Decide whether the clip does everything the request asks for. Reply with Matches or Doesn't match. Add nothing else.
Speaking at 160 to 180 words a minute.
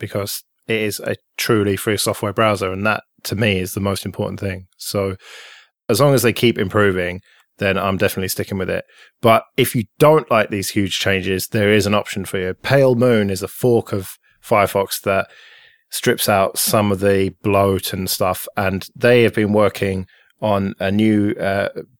Doesn't match